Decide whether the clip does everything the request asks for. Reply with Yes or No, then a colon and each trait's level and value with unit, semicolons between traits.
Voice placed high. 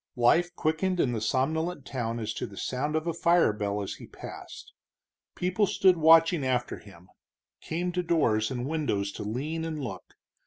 No: medium, 150 Hz